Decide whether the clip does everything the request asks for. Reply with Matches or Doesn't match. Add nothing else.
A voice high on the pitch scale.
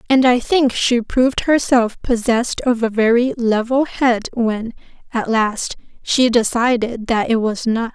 Matches